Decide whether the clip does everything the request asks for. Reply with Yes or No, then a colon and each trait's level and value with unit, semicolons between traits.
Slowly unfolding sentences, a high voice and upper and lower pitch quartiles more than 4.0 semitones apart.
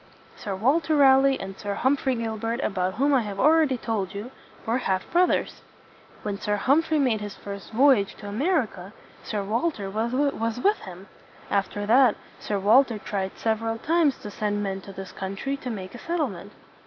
No: average, 190 wpm; high, 225 Hz; average, 5.2 semitones